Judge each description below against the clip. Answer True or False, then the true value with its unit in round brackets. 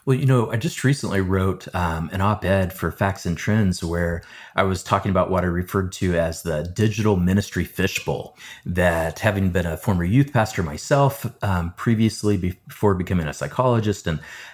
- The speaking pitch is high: False (95 Hz)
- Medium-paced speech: True (185 wpm)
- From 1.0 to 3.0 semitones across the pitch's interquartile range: False (3.4 semitones)